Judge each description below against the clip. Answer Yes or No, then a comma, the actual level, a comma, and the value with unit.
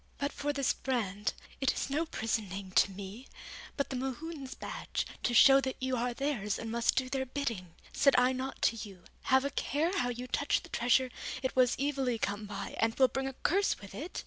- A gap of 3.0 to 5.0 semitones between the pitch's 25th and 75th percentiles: Yes, average, 3.5 semitones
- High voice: Yes, very high, 255 Hz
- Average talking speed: No, fast, 215 wpm